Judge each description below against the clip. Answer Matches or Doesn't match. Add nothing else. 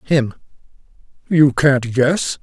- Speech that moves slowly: Matches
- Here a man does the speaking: Matches